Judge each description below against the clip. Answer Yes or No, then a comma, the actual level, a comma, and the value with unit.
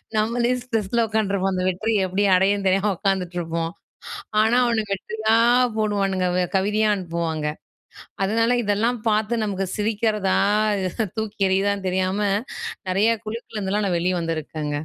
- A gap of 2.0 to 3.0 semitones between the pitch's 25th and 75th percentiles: Yes, average, 2.7 semitones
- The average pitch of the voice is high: Yes, high, 200 Hz